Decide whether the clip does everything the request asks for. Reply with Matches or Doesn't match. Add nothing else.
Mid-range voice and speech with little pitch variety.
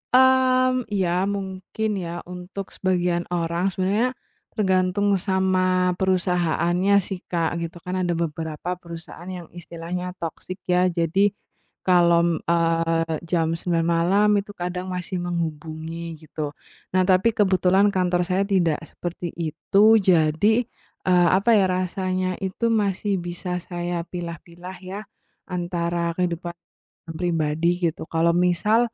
Matches